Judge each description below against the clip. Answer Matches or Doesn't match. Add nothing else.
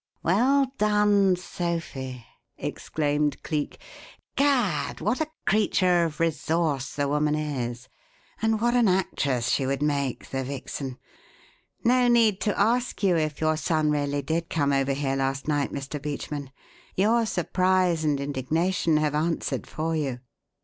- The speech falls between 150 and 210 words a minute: Doesn't match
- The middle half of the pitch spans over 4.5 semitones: Matches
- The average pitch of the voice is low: Doesn't match